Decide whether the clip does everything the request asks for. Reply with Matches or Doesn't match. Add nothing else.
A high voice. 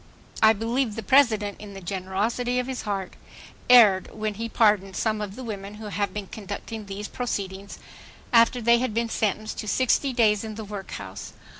Matches